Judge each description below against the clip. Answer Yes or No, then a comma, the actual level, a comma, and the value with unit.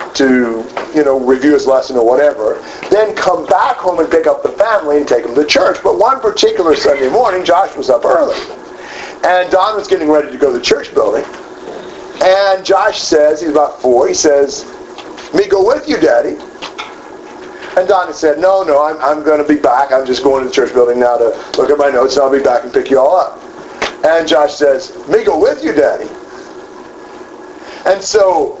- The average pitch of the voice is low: No, medium, 180 Hz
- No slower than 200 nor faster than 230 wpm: Yes, fast, 205 wpm